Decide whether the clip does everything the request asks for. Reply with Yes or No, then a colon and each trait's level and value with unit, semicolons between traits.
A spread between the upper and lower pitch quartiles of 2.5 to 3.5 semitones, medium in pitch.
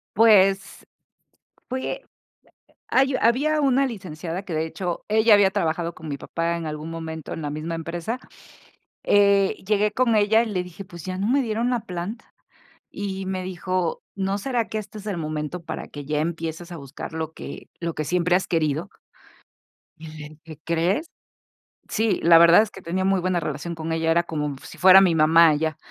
No: average, 4.1 semitones; medium, 180 Hz